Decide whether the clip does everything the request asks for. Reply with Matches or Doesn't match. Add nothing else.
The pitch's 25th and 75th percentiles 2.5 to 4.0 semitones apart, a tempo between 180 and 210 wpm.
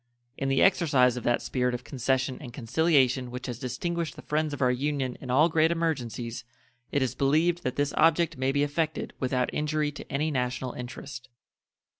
Matches